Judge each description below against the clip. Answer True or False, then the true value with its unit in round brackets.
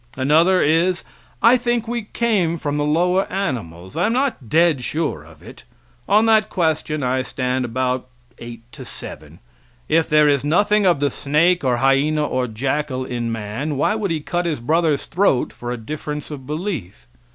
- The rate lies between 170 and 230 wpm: True (175 wpm)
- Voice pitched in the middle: True (150 Hz)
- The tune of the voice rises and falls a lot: True (5.8 semitones)